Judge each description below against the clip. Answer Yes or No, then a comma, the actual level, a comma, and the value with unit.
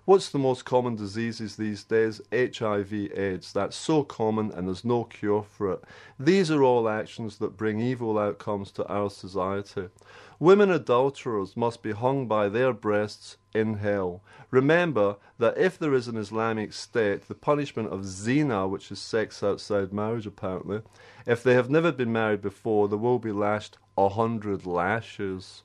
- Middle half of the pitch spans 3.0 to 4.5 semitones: Yes, average, 3.4 semitones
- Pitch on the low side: Yes, low, 110 Hz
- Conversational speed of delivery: Yes, average, 165 wpm